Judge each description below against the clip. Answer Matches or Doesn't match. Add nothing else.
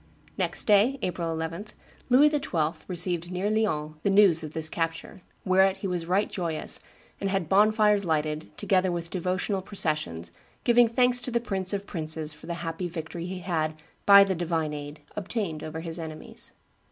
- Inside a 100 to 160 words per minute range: Doesn't match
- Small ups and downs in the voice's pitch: Doesn't match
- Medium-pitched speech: Matches